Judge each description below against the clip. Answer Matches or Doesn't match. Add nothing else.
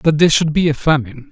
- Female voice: Doesn't match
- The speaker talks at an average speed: Doesn't match